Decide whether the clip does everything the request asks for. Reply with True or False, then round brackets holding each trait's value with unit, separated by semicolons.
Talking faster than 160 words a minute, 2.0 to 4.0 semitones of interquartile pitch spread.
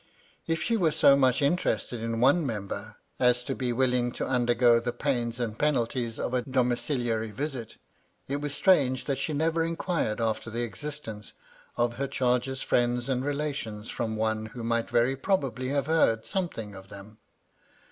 True (170 wpm; 3.5 semitones)